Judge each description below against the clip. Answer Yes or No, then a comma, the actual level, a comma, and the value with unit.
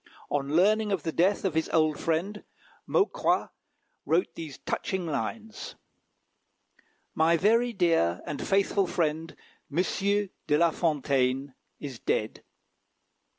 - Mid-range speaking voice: Yes, medium, 165 Hz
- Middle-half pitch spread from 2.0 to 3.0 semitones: No, average, 4.9 semitones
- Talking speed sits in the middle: No, slow, 115 wpm